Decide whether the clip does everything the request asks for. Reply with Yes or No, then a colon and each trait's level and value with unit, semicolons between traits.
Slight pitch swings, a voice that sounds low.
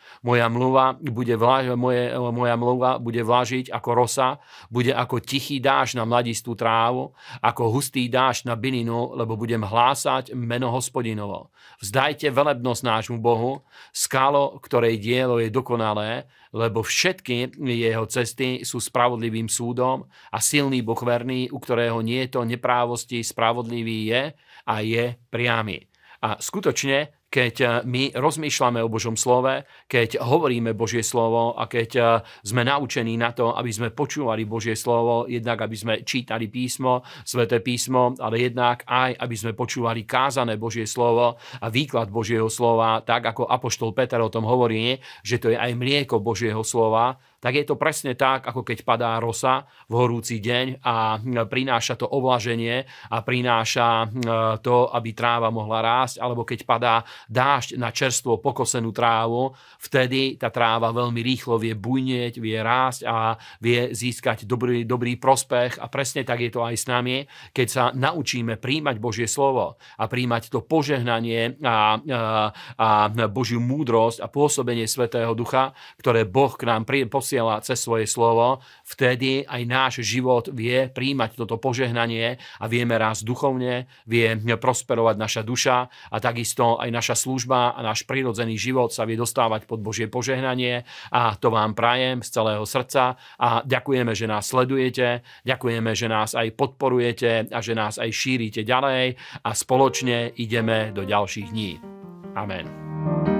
Yes: narrow, 2.0 semitones; low, 120 Hz